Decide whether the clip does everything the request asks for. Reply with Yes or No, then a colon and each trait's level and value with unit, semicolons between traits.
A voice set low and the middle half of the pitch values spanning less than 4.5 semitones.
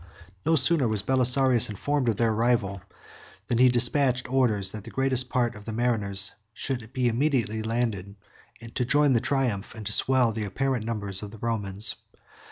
Yes: low, 120 Hz; average, 3.5 semitones